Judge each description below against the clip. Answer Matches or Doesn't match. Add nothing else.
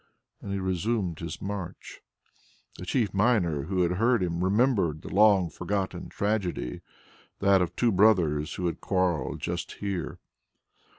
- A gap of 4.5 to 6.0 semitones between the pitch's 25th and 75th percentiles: Doesn't match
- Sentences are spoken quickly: Doesn't match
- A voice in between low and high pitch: Doesn't match